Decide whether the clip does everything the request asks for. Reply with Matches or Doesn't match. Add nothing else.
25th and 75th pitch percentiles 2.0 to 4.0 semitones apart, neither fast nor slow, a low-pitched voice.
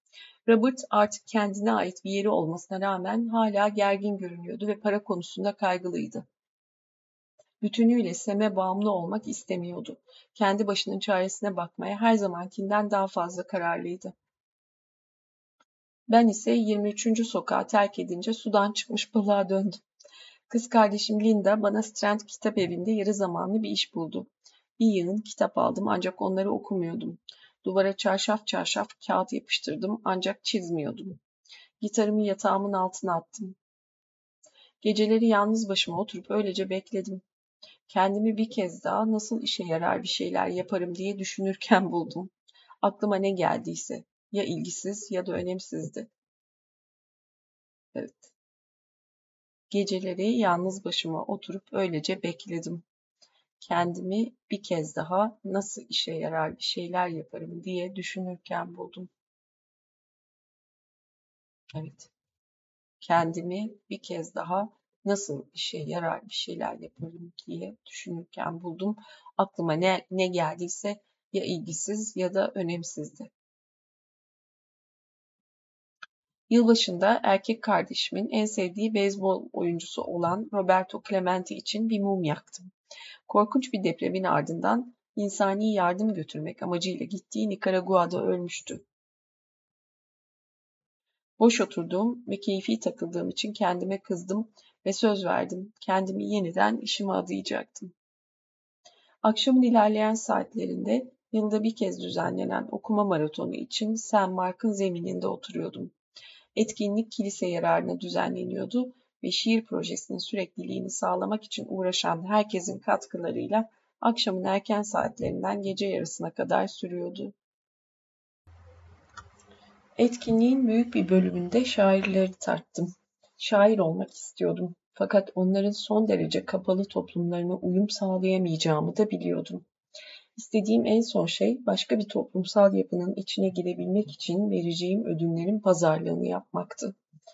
Doesn't match